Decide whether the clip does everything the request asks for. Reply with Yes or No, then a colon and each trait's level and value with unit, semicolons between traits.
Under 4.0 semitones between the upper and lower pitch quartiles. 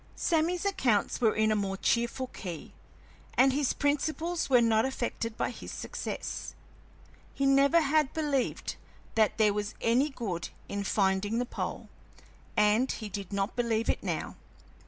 No: average, 4.8 semitones